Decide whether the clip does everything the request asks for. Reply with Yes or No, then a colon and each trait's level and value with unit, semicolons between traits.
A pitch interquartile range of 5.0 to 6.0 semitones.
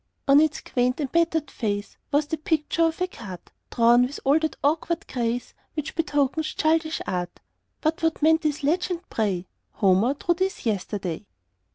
Yes: wide, 5.5 semitones